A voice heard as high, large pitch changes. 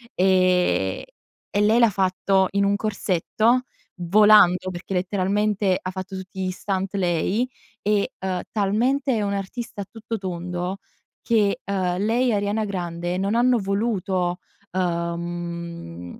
No: high, 195 Hz; narrow, 2.6 semitones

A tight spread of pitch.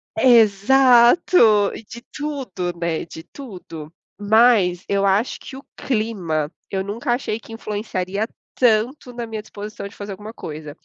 No: average, 4.0 semitones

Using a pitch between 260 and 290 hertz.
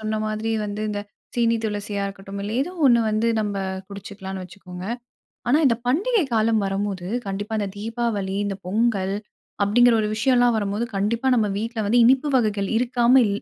No: high, 215 Hz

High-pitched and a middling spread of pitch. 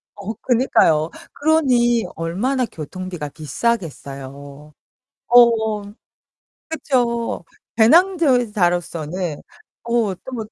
No: high, 220 Hz; wide, 6.6 semitones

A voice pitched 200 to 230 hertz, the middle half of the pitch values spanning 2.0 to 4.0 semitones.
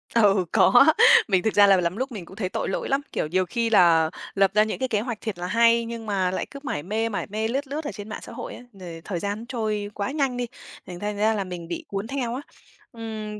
Yes: high, 210 Hz; average, 3.5 semitones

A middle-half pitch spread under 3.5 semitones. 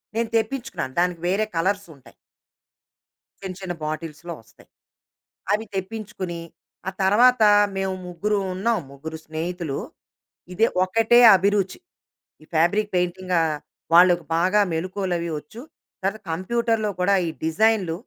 No: average, 3.8 semitones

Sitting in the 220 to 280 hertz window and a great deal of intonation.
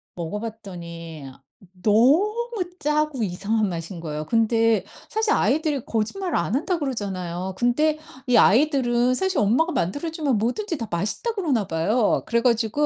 Yes: high, 230 Hz; wide, 7.6 semitones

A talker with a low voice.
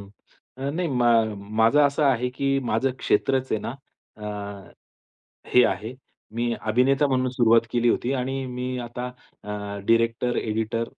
Yes: low, 120 Hz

